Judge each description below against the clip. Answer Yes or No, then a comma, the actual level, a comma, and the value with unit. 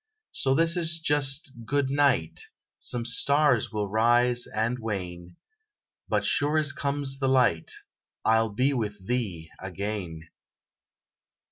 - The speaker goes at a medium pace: No, slow, 120 wpm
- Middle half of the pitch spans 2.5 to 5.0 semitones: No, wide, 5.4 semitones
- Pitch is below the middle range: Yes, low, 120 Hz